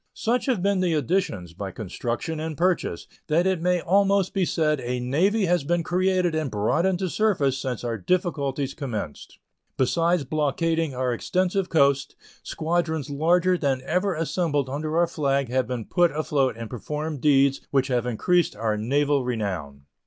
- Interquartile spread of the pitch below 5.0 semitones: No, wide, 5.5 semitones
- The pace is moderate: Yes, average, 165 wpm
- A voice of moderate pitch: Yes, medium, 150 Hz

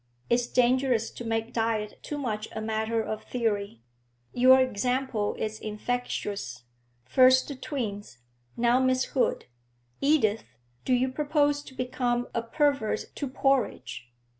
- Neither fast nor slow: No, slow, 130 wpm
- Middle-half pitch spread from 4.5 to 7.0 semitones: No, average, 3.2 semitones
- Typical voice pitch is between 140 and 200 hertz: No, high, 240 Hz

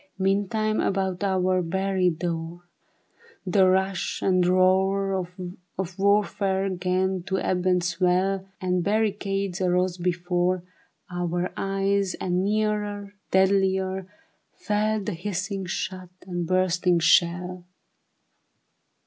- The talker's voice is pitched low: No, medium, 185 Hz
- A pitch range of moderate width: No, narrow, 1.5 semitones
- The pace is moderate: No, slow, 100 wpm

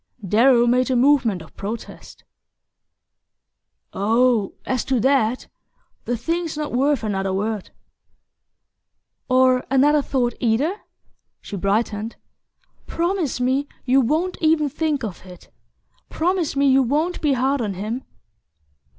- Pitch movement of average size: Yes, average, 4.6 semitones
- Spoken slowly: Yes, slow, 120 wpm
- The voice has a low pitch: No, very high, 255 Hz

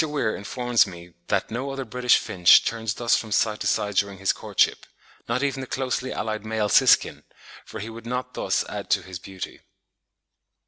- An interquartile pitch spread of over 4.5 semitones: No, average, 3.8 semitones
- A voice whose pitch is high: No, low, 110 Hz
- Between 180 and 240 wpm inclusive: Yes, average, 185 wpm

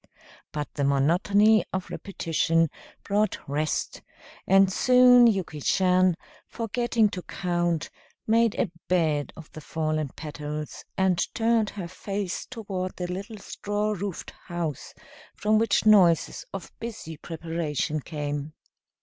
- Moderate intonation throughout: Yes, average, 4.8 semitones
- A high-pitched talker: No, medium, 180 Hz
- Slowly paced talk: Yes, slow, 120 wpm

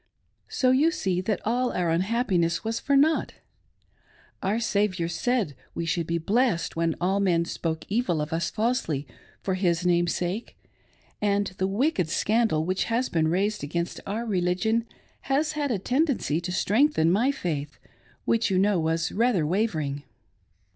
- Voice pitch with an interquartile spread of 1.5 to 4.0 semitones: No, wide, 5.6 semitones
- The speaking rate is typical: Yes, average, 155 wpm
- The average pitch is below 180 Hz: No, high, 190 Hz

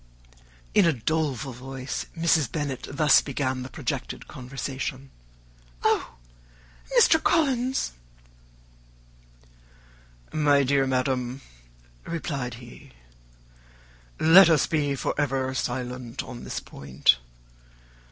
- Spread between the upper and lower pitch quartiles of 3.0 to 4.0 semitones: Yes, average, 3.3 semitones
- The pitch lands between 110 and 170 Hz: Yes, low, 135 Hz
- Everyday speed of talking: No, slow, 95 wpm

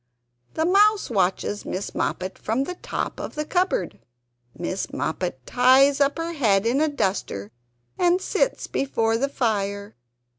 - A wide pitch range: Yes, wide, 7.8 semitones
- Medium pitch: No, very high, 250 Hz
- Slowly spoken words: No, average, 145 wpm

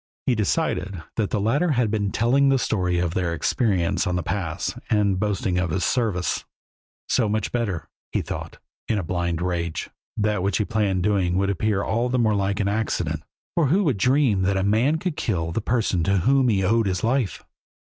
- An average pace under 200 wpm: No, fast, 205 wpm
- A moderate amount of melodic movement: Yes, average, 4.2 semitones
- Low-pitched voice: Yes, low, 100 Hz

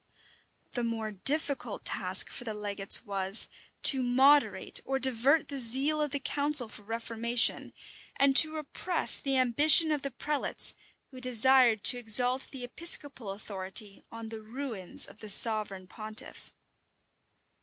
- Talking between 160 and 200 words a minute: No, average, 145 wpm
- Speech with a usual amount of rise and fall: Yes, average, 4.3 semitones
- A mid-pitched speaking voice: No, high, 245 Hz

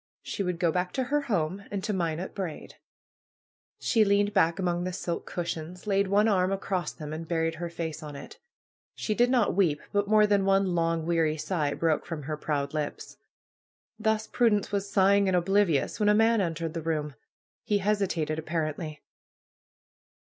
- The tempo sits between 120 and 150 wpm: No, average, 180 wpm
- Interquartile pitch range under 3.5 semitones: No, average, 4.0 semitones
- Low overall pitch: No, medium, 180 Hz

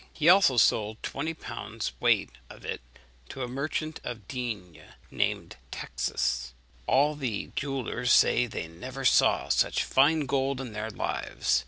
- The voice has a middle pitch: No, low, 125 Hz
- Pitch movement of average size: Yes, average, 4.4 semitones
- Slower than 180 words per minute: Yes, average, 145 wpm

